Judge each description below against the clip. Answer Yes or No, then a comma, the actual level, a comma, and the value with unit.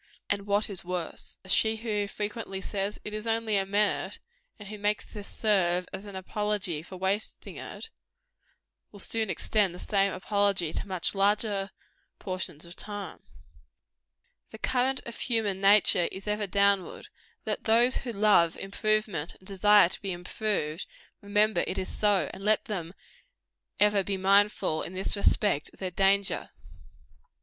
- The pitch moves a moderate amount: No, narrow, 1.9 semitones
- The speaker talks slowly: No, average, 155 wpm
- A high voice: Yes, high, 200 Hz